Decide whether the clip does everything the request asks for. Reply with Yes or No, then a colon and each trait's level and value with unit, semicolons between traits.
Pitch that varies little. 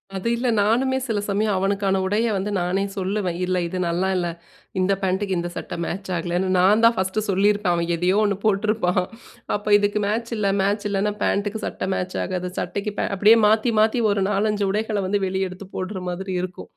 Yes: narrow, 2.2 semitones